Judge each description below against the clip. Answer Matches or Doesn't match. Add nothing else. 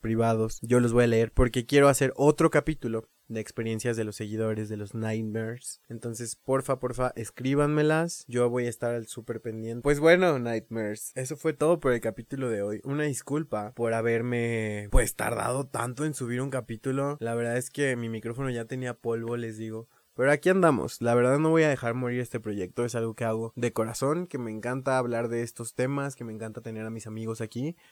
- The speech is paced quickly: Matches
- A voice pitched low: Matches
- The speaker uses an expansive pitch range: Doesn't match